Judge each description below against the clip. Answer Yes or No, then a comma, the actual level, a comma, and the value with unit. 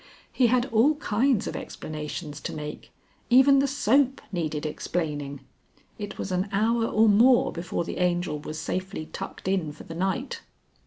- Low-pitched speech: No, high, 190 Hz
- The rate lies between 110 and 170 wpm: Yes, average, 160 wpm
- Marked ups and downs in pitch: Yes, wide, 7.3 semitones